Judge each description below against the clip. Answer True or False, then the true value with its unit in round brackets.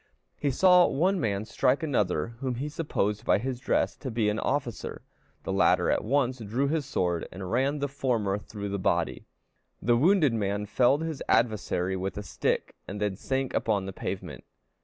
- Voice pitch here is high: False (120 Hz)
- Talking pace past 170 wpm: True (180 wpm)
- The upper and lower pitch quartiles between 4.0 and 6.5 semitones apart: True (5.5 semitones)